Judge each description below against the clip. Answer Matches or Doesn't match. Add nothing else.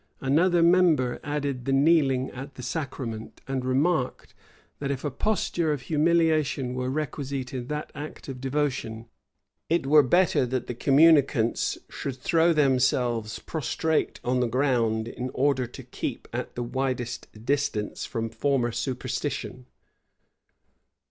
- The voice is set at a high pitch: Doesn't match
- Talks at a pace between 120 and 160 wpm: Matches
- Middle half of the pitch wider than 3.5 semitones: Doesn't match